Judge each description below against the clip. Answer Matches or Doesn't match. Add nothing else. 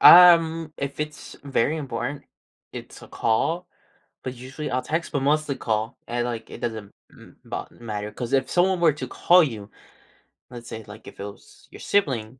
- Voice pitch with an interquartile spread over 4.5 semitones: Matches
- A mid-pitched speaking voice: Doesn't match